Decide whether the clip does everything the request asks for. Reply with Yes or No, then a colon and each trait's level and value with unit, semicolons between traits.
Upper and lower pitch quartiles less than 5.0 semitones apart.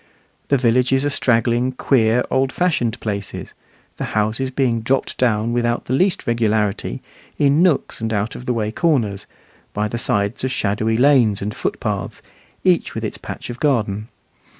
Yes: average, 3.5 semitones